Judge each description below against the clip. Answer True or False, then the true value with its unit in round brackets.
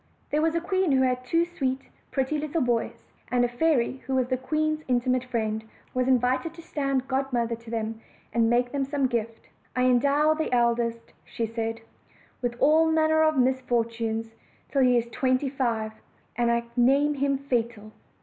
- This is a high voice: True (255 Hz)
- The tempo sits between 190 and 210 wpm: False (175 wpm)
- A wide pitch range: False (3.1 semitones)